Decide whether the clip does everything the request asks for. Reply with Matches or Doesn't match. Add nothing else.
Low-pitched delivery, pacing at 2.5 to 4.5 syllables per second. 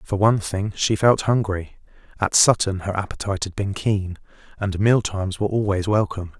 Doesn't match